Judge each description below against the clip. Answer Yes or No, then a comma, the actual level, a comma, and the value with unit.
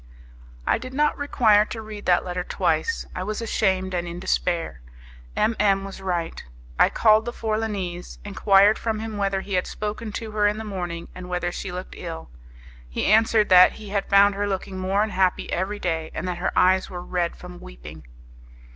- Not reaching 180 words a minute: No, average, 190 wpm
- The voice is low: No, high, 195 Hz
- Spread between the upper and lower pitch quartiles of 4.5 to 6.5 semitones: No, average, 3.0 semitones